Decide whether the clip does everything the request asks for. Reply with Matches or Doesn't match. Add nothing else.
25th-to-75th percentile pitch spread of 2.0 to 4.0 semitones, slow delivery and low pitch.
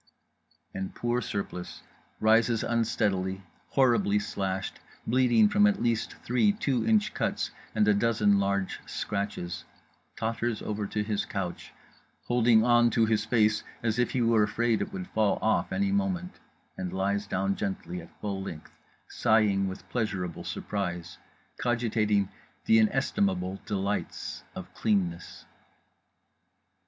Matches